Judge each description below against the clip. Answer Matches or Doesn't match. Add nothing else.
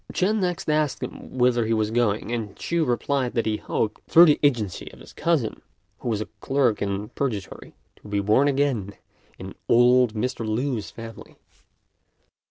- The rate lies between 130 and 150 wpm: Doesn't match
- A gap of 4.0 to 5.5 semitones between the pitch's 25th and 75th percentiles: Matches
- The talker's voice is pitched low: Matches